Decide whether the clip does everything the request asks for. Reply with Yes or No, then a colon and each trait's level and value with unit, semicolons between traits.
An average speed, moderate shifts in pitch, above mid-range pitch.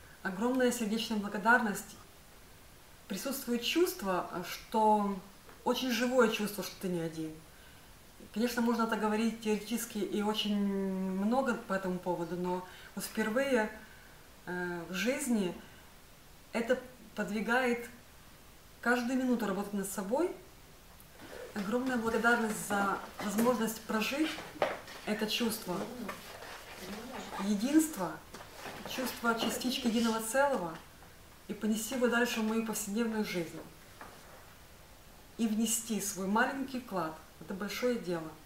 No: slow, 100 wpm; average, 3.8 semitones; high, 215 Hz